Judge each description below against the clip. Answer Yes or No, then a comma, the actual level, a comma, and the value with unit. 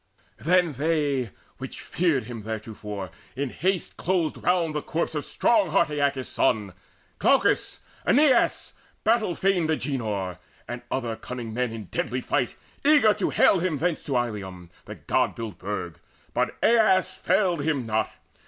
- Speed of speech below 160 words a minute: Yes, average, 145 wpm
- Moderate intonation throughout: No, wide, 8.0 semitones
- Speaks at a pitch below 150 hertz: Yes, medium, 140 Hz